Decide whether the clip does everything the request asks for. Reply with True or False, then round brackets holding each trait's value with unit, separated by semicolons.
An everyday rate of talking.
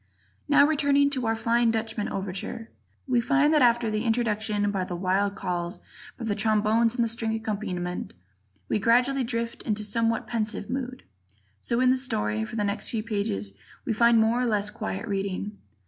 True (180 wpm)